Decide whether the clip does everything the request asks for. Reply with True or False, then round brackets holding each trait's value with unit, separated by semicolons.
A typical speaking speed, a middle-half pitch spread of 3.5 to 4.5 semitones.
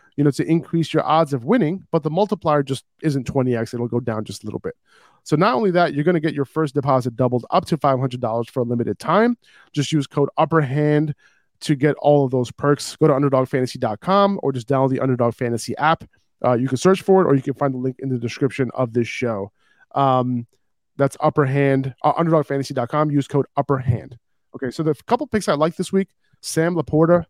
False (215 wpm; 3.9 semitones)